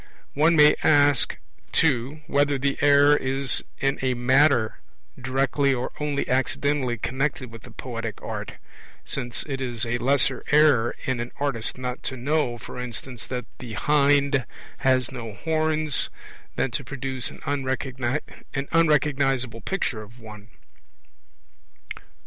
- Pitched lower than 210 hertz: Yes, low, 135 Hz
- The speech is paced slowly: Yes, slow, 130 wpm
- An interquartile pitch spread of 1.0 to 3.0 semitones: Yes, average, 2.7 semitones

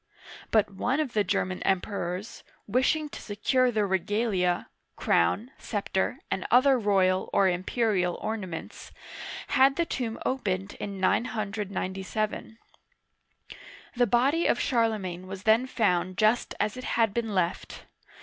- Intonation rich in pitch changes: No, average, 4.1 semitones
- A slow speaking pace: Yes, slow, 125 wpm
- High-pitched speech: Yes, high, 210 Hz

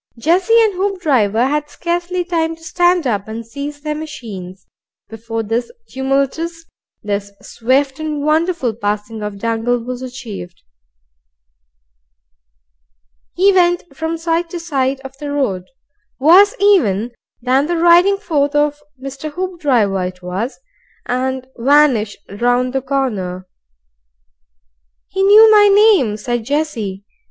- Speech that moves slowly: Yes, slow, 125 wpm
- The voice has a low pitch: No, very high, 275 Hz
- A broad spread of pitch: Yes, wide, 6.7 semitones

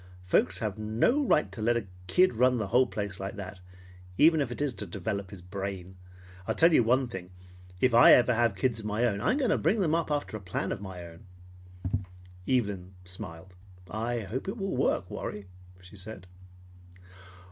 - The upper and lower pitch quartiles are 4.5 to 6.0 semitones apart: Yes, average, 5.0 semitones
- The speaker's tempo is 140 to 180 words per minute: No, average, 200 wpm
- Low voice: Yes, low, 110 Hz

